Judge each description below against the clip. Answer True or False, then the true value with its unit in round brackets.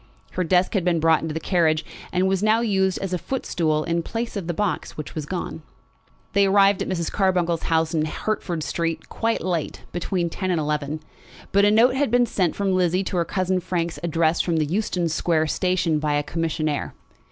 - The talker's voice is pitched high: False (175 Hz)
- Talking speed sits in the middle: False (210 wpm)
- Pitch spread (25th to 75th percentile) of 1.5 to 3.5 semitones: True (3.1 semitones)